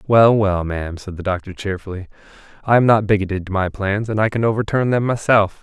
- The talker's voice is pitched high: No, low, 100 Hz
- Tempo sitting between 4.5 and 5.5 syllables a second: No, 5.9 syllables/s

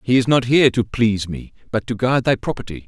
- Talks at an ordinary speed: No, fast, 250 wpm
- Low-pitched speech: Yes, low, 120 Hz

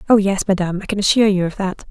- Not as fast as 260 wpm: No, fast, 285 wpm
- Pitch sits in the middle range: No, high, 195 Hz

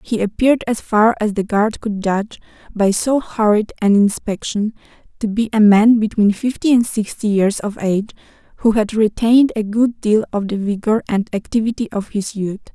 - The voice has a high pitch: Yes, high, 215 Hz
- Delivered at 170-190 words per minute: Yes, average, 185 wpm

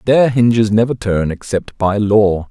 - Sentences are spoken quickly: No, average, 170 wpm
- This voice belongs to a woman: No, male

